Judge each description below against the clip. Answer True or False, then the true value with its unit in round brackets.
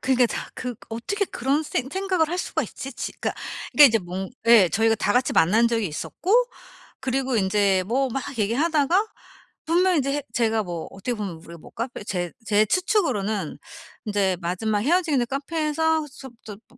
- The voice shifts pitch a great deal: True (6.4 semitones)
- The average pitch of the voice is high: True (240 Hz)